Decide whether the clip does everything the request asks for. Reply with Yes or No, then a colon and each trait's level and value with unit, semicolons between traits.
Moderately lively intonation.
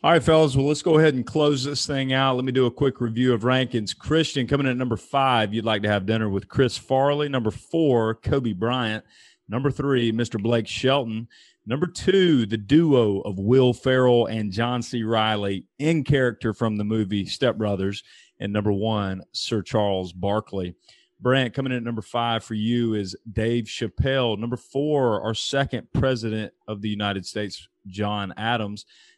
Yes: average, 3.8 semitones